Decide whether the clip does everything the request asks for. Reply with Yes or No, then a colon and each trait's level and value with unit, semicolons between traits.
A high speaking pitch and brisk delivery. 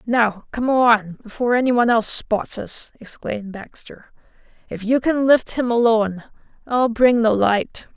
No: high, 230 Hz; average, 150 wpm